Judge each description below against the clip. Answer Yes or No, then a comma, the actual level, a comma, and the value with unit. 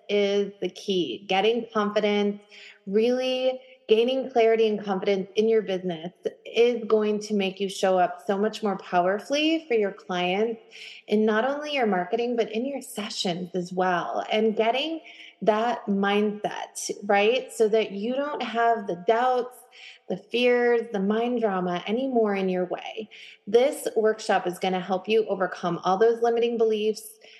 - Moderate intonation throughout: Yes, average, 3.1 semitones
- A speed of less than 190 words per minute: Yes, average, 155 wpm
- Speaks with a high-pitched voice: Yes, high, 215 Hz